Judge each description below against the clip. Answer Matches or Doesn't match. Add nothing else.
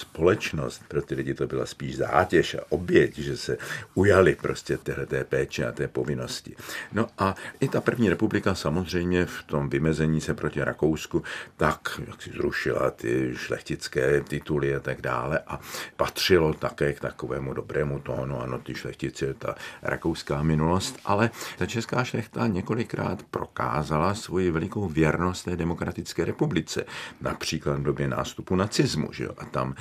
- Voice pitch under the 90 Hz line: Matches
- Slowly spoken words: Doesn't match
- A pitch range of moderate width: Matches